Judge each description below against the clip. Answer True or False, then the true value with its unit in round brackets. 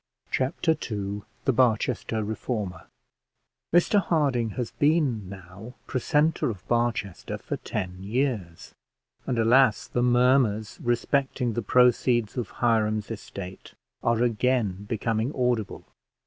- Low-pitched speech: True (115 Hz)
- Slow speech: True (110 wpm)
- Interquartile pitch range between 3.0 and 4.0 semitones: True (3.4 semitones)